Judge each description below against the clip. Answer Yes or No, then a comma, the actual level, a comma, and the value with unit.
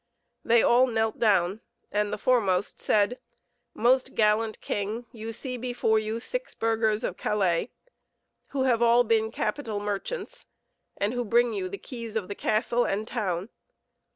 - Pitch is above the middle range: Yes, high, 220 Hz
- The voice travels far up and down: No, narrow, 2.5 semitones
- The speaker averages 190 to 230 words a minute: No, average, 155 wpm